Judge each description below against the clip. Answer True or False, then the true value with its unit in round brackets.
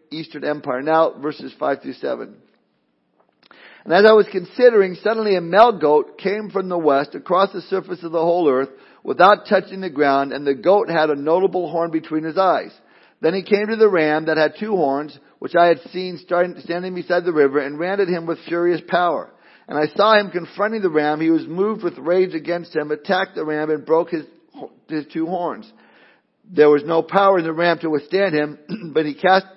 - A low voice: False (170 Hz)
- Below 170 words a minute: False (205 wpm)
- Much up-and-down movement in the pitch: False (3.7 semitones)